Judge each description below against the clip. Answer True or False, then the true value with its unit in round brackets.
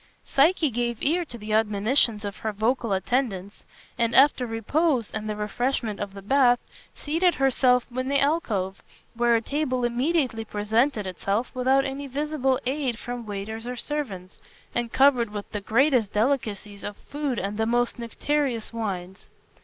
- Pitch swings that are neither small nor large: True (4.3 semitones)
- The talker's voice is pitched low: False (240 Hz)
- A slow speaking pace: False (155 wpm)